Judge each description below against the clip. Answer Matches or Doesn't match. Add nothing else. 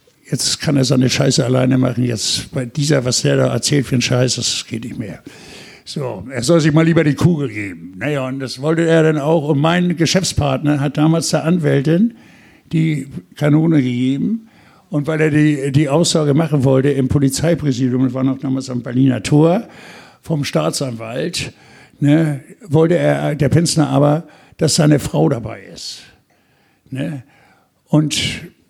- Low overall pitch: Doesn't match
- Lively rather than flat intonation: Doesn't match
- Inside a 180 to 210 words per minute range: Doesn't match